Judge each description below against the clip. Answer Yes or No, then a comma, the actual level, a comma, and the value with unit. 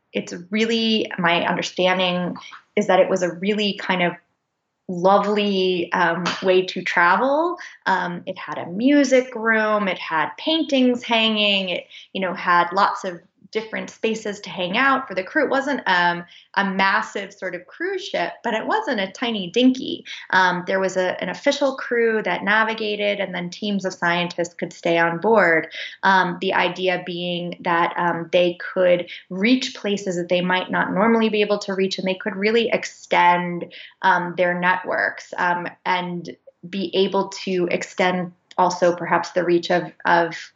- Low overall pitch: No, medium, 185 Hz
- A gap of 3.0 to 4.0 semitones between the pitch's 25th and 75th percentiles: Yes, average, 3.5 semitones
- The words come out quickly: No, average, 165 wpm